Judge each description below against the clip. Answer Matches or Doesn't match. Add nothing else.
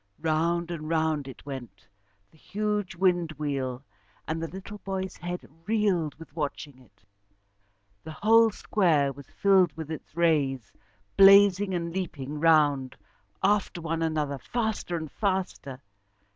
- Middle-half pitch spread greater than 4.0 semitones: Matches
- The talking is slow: Matches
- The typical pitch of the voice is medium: Matches